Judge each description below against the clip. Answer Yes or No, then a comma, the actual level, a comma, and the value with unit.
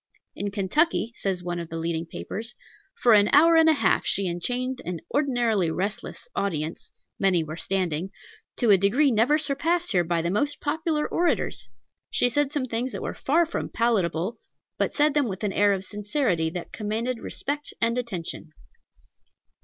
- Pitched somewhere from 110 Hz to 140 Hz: No, high, 215 Hz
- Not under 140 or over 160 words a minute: No, average, 170 wpm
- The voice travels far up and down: Yes, wide, 7.6 semitones